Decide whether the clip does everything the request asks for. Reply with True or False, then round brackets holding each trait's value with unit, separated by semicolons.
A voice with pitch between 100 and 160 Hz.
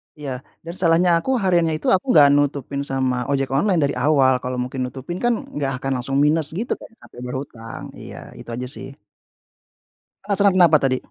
True (140 Hz)